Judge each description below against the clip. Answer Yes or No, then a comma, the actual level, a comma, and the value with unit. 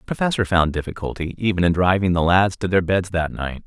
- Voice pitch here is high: No, very low, 90 Hz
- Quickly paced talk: Yes, fast, 230 wpm